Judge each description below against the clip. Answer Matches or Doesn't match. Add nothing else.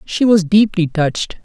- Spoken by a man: Matches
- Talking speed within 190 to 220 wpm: Doesn't match